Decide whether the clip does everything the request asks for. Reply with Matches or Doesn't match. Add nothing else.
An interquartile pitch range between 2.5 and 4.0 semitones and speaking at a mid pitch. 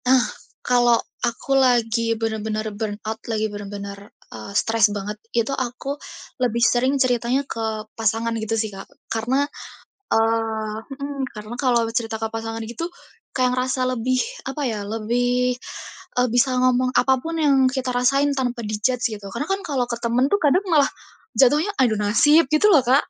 Doesn't match